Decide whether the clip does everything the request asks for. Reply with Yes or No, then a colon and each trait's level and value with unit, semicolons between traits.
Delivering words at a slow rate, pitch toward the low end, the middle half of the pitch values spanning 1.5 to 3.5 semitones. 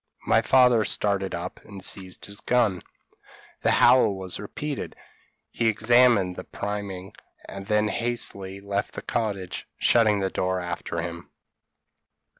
Yes: slow, 130 wpm; low, 100 Hz; average, 3.1 semitones